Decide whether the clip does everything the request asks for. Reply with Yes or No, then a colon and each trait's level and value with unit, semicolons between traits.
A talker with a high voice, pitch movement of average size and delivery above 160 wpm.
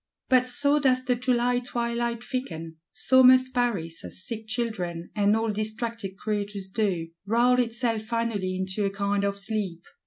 No: high, 220 Hz; average, 3.6 semitones; average, 155 wpm